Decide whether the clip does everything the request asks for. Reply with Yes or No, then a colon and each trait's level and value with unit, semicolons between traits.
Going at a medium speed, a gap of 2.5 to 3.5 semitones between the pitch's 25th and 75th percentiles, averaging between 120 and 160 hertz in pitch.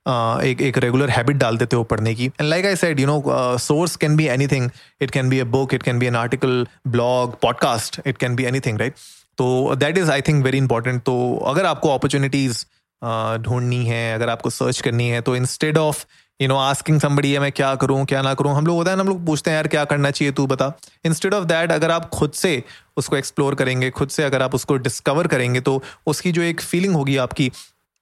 No: fast, 235 wpm; average, 3.2 semitones; low, 135 Hz